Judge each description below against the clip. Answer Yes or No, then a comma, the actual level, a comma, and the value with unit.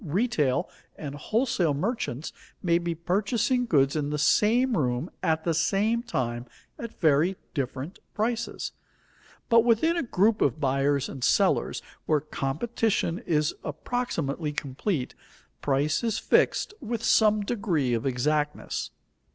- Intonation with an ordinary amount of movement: No, wide, 7.7 semitones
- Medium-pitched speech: Yes, medium, 165 Hz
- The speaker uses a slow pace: Yes, slow, 125 wpm